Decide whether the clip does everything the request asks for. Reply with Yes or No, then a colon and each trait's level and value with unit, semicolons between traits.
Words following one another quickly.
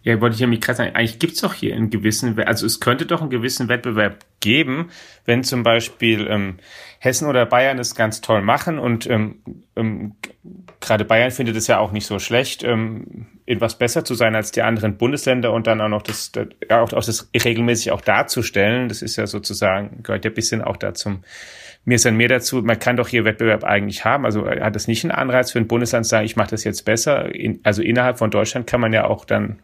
Yes: fast, 235 wpm